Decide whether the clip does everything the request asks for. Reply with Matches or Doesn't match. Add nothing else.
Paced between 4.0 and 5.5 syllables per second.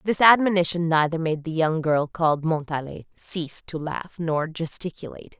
Matches